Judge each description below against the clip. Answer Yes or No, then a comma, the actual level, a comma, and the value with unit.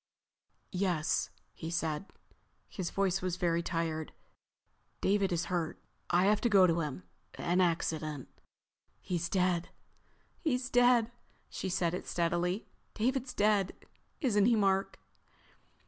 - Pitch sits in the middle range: Yes, medium, 180 Hz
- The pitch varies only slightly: No, average, 3.4 semitones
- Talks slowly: Yes, slow, 115 wpm